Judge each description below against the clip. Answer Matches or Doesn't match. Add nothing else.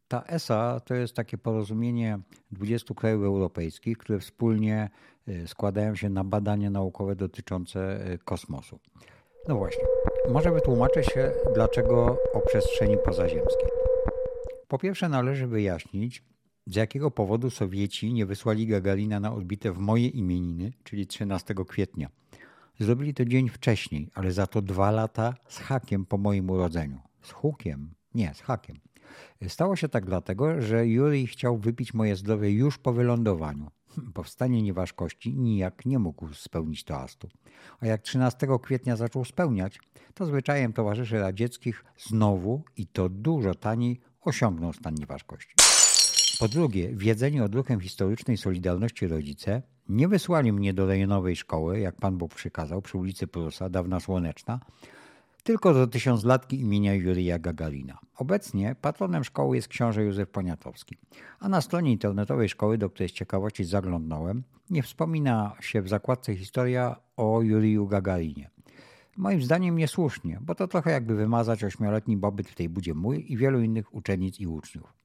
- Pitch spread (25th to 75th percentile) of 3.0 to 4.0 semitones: Doesn't match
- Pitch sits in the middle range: Doesn't match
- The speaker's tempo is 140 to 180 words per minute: Matches